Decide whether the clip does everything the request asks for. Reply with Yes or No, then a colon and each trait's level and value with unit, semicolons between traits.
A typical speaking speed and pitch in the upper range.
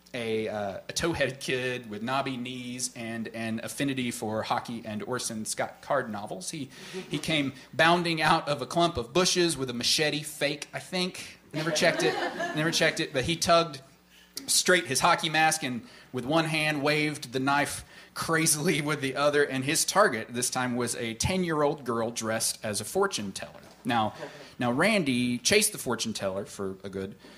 No: average, 180 wpm; low, 135 Hz